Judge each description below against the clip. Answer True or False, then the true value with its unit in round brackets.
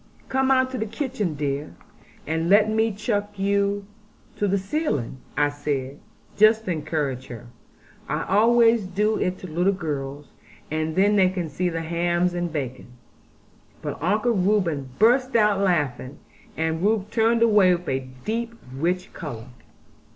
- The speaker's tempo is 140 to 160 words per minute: True (150 wpm)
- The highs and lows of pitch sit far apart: True (5.7 semitones)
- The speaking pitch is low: False (185 Hz)